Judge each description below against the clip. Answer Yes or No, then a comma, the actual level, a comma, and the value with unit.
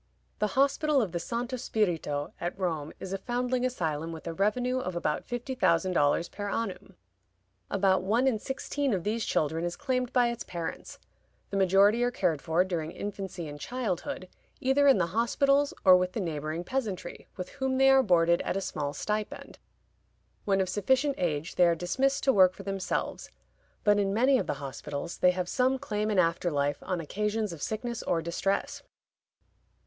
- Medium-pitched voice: No, high, 195 Hz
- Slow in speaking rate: No, average, 185 wpm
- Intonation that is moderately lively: No, wide, 6.1 semitones